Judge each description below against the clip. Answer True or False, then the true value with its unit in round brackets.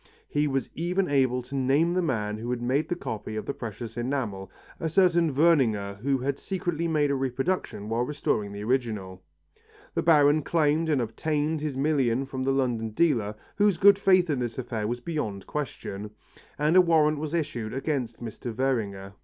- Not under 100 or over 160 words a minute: False (180 wpm)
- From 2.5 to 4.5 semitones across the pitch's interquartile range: False (5.2 semitones)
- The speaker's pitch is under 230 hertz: True (135 Hz)